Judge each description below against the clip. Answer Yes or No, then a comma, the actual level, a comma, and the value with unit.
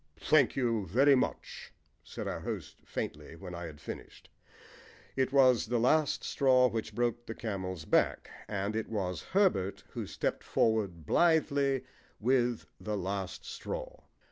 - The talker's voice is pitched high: No, low, 115 Hz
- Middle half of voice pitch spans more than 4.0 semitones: Yes, wide, 5.6 semitones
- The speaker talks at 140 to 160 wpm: Yes, average, 145 wpm